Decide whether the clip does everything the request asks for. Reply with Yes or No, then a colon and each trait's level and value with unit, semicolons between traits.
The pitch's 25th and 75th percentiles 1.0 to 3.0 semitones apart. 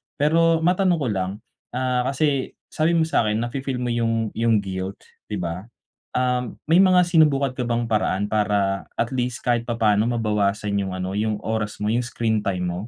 No: average, 4.2 semitones